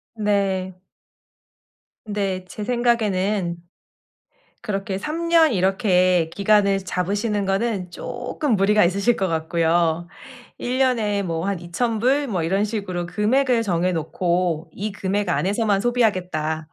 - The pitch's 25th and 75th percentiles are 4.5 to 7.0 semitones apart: No, average, 3.5 semitones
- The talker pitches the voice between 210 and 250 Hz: No, high, 195 Hz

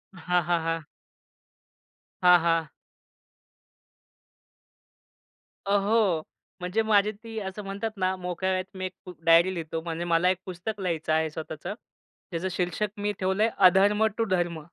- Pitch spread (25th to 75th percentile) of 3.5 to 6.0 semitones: No, average, 3.1 semitones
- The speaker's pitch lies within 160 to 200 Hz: Yes, medium, 185 Hz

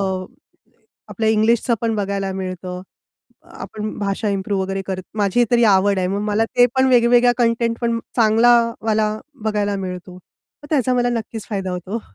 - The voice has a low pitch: No, high, 215 Hz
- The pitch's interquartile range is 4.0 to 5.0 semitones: No, average, 3.3 semitones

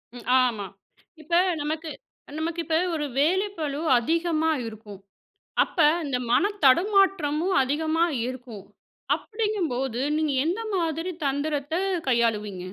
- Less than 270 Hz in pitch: No, very high, 305 Hz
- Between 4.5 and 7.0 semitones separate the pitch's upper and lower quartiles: Yes, average, 4.9 semitones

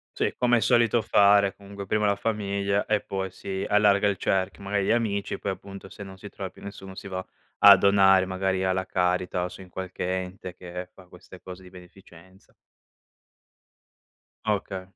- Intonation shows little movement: Yes, narrow, 1.4 semitones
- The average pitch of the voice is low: Yes, very low, 95 Hz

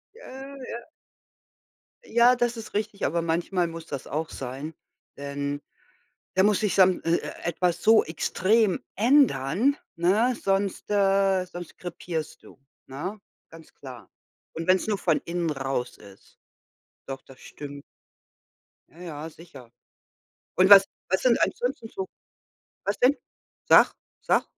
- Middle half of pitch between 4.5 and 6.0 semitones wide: Yes, wide, 5.6 semitones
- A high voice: No, medium, 180 Hz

